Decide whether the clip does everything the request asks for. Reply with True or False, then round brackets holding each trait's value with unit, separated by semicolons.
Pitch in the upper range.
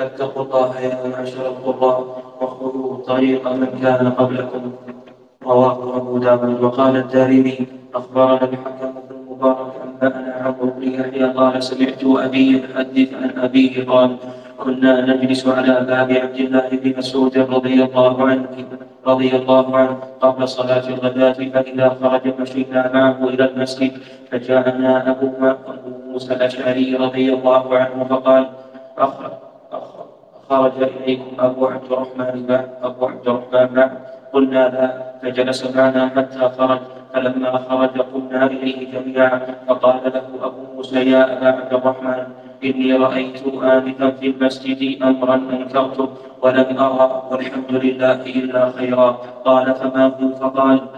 False (130 Hz)